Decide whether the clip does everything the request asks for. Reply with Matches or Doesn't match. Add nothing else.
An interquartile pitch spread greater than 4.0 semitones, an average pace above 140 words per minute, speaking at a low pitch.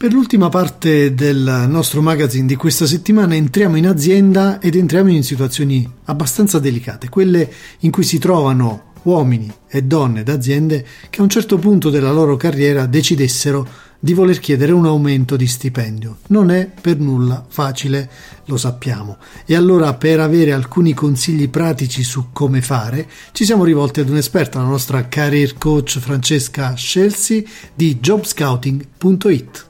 Doesn't match